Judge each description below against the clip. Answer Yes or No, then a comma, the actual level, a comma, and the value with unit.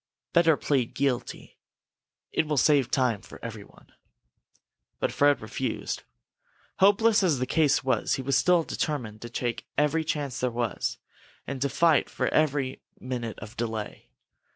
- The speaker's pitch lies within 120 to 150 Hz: Yes, low, 135 Hz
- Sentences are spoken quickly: No, average, 145 wpm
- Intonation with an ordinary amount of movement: Yes, average, 4.2 semitones